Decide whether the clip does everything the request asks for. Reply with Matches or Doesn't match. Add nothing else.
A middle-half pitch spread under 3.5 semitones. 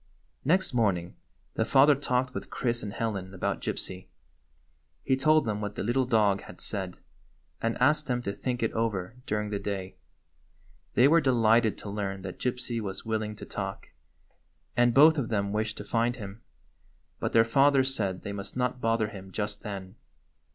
Doesn't match